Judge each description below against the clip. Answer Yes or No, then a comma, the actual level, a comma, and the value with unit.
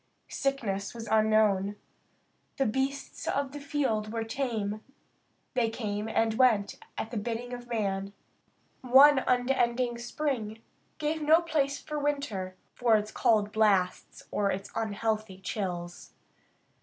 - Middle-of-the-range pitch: No, high, 225 Hz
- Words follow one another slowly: Yes, slow, 125 wpm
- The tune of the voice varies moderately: Yes, average, 4.2 semitones